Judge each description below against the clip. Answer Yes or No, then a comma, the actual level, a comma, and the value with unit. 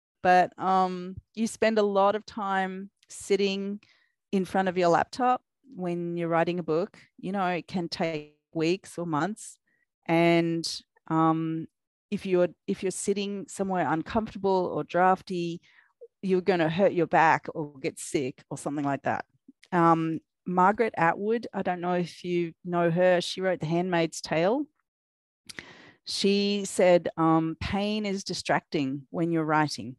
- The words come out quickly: No, average, 150 wpm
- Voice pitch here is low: No, medium, 180 Hz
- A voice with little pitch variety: No, average, 3.1 semitones